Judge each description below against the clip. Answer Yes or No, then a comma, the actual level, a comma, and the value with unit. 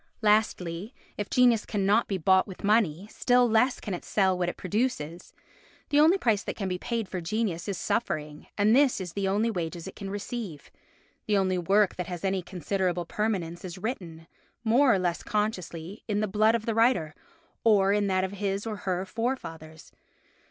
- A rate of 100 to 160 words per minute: No, average, 185 wpm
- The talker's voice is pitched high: Yes, high, 200 Hz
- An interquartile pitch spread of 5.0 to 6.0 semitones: No, average, 3.6 semitones